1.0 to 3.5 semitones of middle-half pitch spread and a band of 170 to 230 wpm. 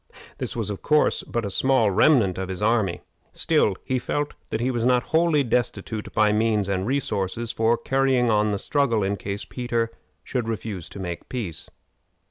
No: average, 3.9 semitones; average, 180 wpm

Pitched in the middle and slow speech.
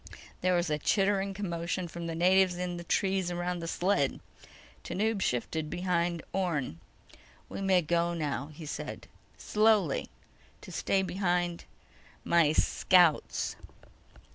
Yes: medium, 175 Hz; slow, 125 wpm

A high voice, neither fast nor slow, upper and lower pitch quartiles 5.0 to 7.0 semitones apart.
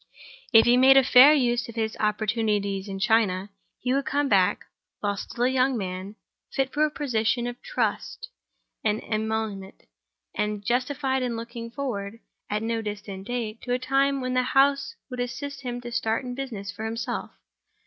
No: high, 235 Hz; average, 175 wpm; average, 3.5 semitones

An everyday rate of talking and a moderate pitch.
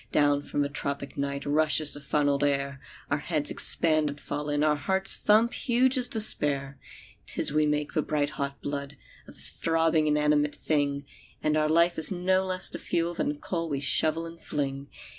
Yes: average, 190 wpm; medium, 150 Hz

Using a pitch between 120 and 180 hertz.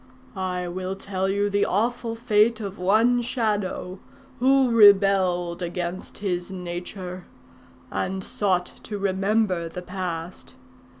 No: high, 190 Hz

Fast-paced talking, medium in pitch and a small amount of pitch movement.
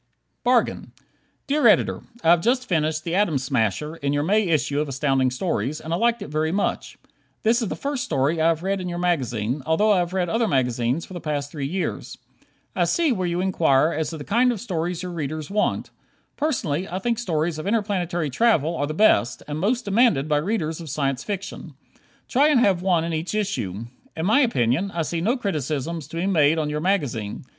No: fast, 210 wpm; medium, 165 Hz; average, 5.3 semitones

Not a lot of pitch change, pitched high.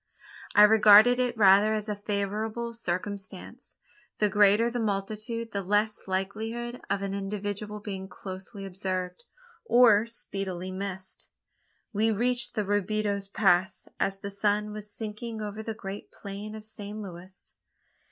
Yes: narrow, 1.8 semitones; high, 205 Hz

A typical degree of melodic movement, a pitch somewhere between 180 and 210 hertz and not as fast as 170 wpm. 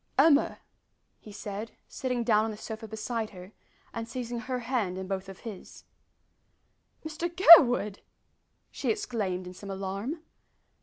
No: average, 4.2 semitones; high, 220 Hz; average, 140 wpm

